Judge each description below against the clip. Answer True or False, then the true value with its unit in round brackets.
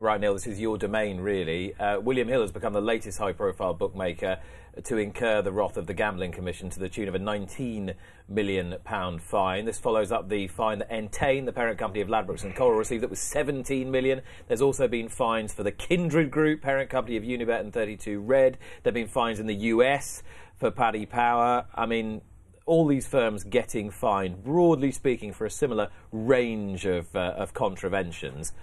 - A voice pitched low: True (110 Hz)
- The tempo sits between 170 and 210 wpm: True (195 wpm)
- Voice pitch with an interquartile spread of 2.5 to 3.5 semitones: False (4.5 semitones)